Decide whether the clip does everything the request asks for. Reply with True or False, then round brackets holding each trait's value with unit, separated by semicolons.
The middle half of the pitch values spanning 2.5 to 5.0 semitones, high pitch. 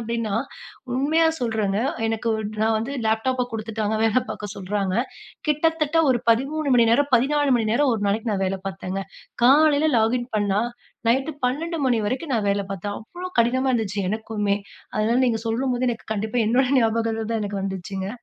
True (3.8 semitones; 230 Hz)